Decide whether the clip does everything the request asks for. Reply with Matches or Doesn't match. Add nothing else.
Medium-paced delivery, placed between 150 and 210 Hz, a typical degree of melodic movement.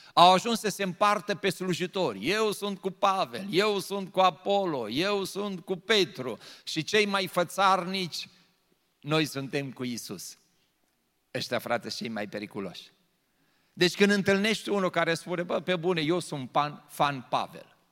Matches